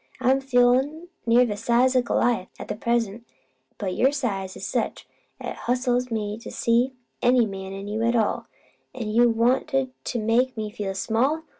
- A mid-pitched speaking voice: No, high, 235 Hz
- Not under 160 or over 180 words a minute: Yes, average, 175 wpm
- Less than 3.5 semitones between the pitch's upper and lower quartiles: Yes, average, 2.9 semitones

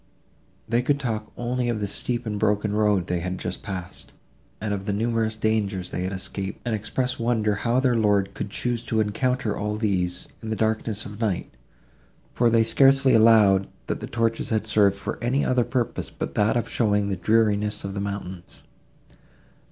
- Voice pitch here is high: No, low, 110 Hz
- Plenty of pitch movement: No, narrow, 2.6 semitones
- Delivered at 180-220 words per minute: Yes, average, 185 wpm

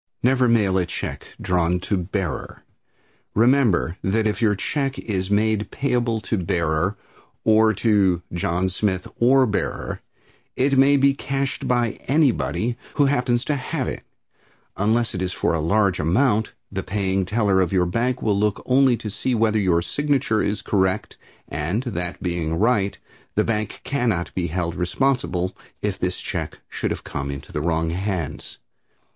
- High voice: No, low, 105 Hz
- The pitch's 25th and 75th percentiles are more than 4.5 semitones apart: Yes, average, 5.2 semitones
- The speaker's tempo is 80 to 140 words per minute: No, average, 160 wpm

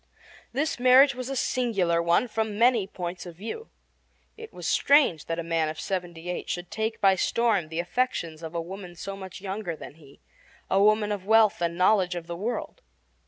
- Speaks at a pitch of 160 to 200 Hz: Yes, high, 190 Hz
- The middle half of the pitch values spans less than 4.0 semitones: No, average, 4.8 semitones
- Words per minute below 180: No, average, 195 wpm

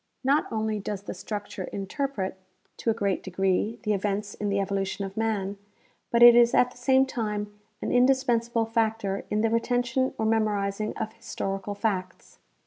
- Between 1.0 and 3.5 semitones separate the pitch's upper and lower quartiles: Yes, average, 2.8 semitones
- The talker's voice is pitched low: No, high, 215 Hz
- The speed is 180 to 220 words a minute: No, average, 170 wpm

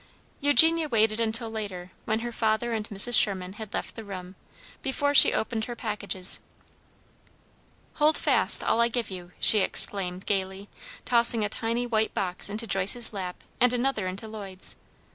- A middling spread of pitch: Yes, average, 3.5 semitones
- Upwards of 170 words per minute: No, average, 160 wpm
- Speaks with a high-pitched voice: Yes, high, 220 Hz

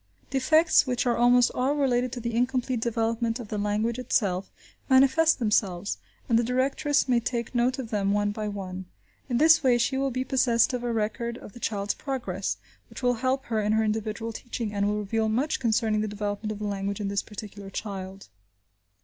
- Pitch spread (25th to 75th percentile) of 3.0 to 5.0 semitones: Yes, average, 3.3 semitones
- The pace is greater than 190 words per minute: Yes, average, 200 wpm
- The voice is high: Yes, high, 230 Hz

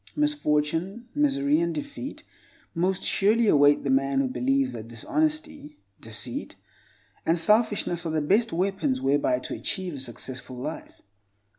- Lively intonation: Yes, wide, 8.1 semitones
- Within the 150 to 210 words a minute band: No, slow, 135 wpm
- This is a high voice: No, medium, 165 Hz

